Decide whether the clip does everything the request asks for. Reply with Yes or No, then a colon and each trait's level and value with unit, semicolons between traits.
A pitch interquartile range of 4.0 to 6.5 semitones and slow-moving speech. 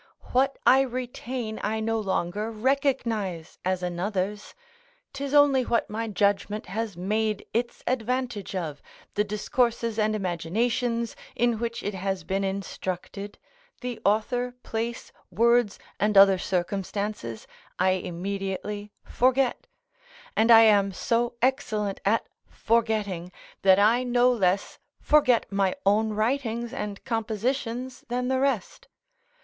No: average, 3.5 semitones; slow, 120 wpm